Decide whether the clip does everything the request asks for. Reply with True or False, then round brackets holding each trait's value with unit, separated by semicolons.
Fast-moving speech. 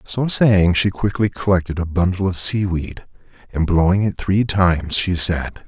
False (180 wpm)